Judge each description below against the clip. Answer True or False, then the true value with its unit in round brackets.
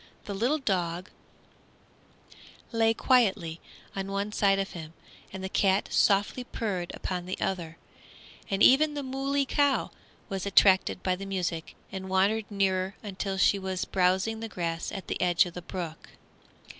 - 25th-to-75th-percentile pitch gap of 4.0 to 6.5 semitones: False (2.8 semitones)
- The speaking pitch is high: True (195 Hz)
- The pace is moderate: True (155 wpm)